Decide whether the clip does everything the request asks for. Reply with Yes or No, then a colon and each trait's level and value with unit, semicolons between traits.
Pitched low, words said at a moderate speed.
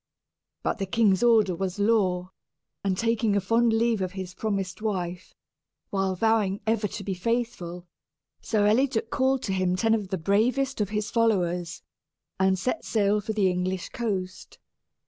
No: high, 200 Hz; average, 160 wpm